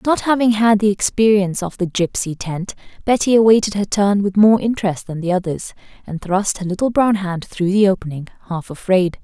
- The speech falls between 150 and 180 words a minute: No, average, 195 wpm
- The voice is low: No, high, 200 Hz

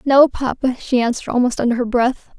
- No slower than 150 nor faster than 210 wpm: Yes, average, 200 wpm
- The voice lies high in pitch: Yes, very high, 250 Hz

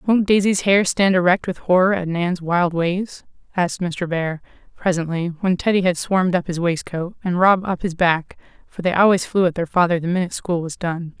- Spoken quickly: Yes, fast, 210 wpm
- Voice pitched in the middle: Yes, medium, 180 Hz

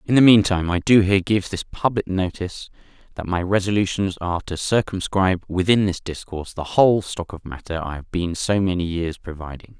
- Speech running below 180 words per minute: No, average, 190 wpm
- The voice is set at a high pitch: No, very low, 95 Hz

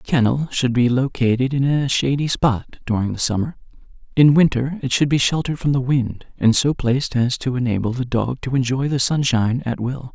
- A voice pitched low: Yes, low, 130 Hz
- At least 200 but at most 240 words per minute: Yes, fast, 205 wpm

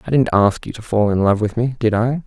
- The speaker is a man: Yes, male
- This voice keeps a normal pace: No, fast, 320 wpm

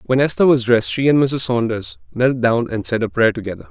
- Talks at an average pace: No, fast, 245 wpm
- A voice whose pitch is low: Yes, low, 125 Hz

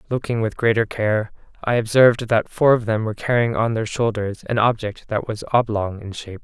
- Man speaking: Yes, male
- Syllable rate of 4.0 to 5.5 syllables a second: Yes, 5.4 syllables/s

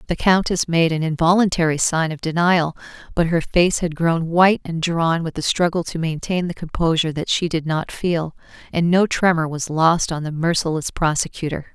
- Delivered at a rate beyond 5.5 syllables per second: No, 5.1 syllables/s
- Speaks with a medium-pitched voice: Yes, medium, 165 Hz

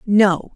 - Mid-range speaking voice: No, high, 195 Hz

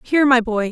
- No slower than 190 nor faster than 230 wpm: No, fast, 250 wpm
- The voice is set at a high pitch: Yes, high, 245 Hz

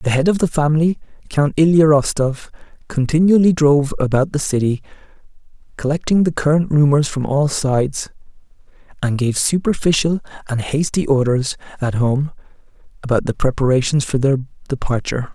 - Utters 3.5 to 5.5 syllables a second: Yes, 5.4 syllables/s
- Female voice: No, male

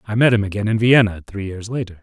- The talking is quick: Yes, fast, 265 wpm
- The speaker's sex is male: Yes, male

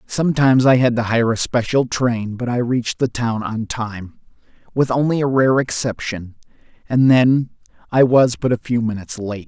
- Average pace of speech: Yes, average, 185 wpm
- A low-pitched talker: Yes, low, 120 Hz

